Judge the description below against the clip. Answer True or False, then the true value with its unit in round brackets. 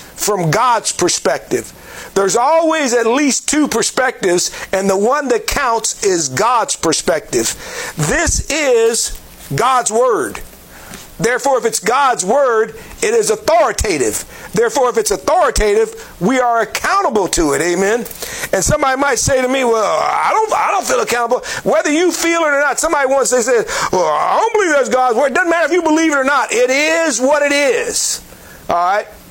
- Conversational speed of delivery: True (175 wpm)